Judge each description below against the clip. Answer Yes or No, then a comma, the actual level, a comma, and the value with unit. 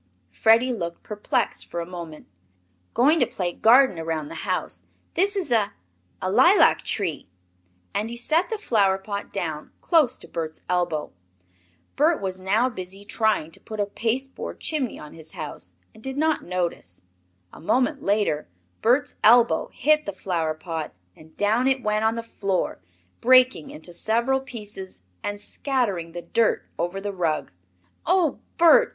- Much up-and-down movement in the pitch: Yes, wide, 6.6 semitones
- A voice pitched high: Yes, high, 210 Hz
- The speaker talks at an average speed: Yes, average, 160 wpm